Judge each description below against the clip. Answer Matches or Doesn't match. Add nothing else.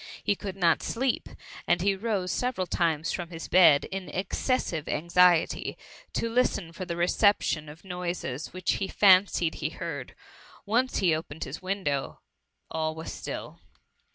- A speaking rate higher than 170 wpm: Doesn't match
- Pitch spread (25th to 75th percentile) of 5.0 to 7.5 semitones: Doesn't match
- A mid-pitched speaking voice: Matches